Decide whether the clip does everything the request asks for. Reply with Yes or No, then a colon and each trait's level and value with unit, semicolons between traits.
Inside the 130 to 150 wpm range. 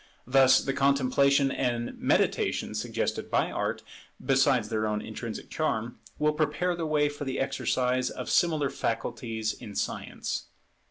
Yes: average, 140 wpm